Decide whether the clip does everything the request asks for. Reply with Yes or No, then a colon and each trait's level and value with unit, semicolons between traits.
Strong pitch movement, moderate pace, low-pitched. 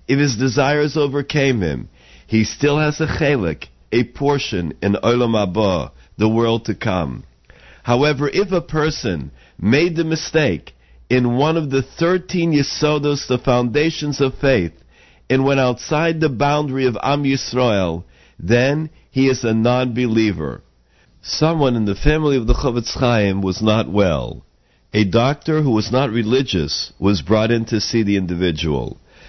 Yes: wide, 6.0 semitones; average, 150 wpm; low, 125 Hz